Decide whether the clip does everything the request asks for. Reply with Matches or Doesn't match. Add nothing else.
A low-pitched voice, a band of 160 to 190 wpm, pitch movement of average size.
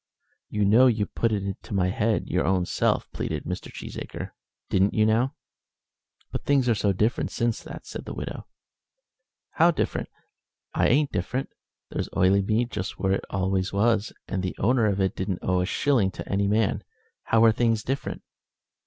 Matches